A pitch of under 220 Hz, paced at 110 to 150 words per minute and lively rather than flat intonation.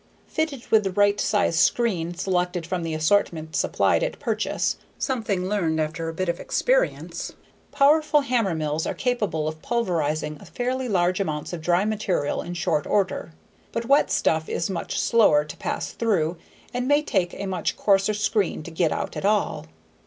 No: high, 190 Hz; average, 165 wpm; wide, 5.7 semitones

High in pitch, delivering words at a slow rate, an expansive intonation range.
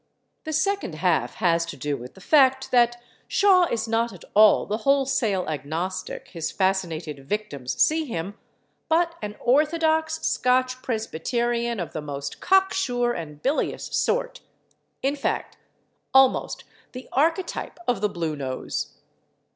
Yes: high, 235 Hz; slow, 130 wpm; wide, 9.0 semitones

